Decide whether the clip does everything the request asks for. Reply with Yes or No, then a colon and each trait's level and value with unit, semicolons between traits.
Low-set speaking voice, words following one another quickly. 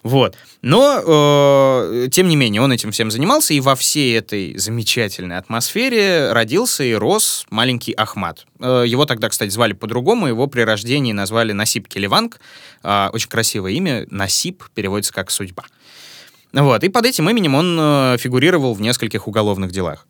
No: low, 120 Hz; average, 150 wpm